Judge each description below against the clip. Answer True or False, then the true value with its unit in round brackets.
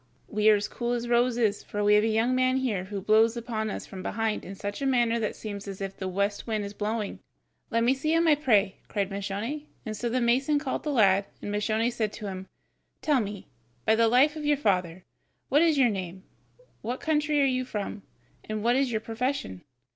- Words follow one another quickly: True (225 wpm)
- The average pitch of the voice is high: True (225 Hz)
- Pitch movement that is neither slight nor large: True (4.0 semitones)